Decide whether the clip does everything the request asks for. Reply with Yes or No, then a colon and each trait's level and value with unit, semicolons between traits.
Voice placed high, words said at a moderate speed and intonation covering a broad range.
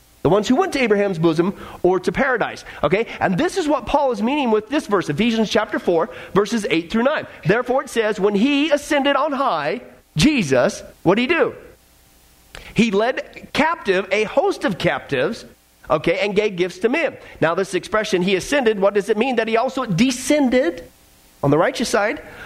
Yes: high, 215 Hz; average, 190 wpm; wide, 6.4 semitones